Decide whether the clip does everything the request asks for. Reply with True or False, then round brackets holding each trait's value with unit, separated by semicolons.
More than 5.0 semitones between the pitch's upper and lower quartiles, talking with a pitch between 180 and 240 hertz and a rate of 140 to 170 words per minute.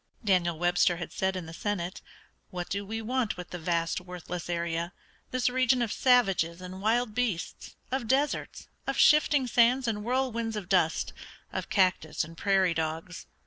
True (5.4 semitones; 190 Hz; 165 wpm)